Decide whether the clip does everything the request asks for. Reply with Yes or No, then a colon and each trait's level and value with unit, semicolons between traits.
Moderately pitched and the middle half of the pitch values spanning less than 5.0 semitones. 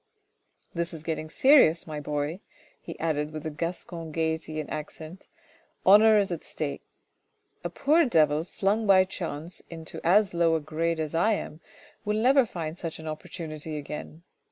Yes: medium, 165 Hz; average, 3.2 semitones